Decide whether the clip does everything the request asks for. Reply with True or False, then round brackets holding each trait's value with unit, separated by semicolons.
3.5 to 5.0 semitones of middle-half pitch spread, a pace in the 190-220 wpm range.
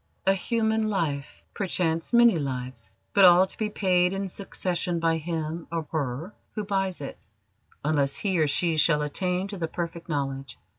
False (4.3 semitones; 165 wpm)